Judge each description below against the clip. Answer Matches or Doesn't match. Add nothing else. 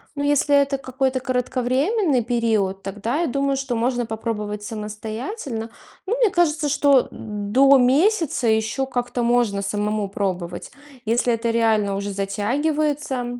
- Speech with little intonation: Doesn't match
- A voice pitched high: Matches